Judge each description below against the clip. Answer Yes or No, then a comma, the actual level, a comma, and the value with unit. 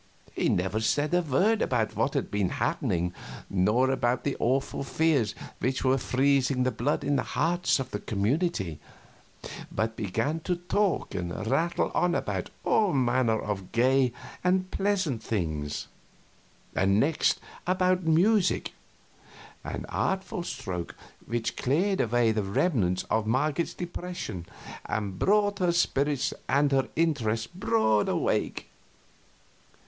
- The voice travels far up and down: Yes, wide, 7.8 semitones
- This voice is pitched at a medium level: No, low, 130 Hz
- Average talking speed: No, slow, 130 wpm